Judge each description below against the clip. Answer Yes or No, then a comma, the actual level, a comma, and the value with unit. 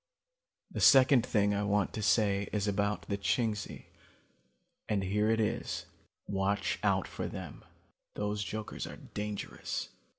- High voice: No, low, 105 Hz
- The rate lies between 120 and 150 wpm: Yes, slow, 135 wpm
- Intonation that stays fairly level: Yes, narrow, 1.1 semitones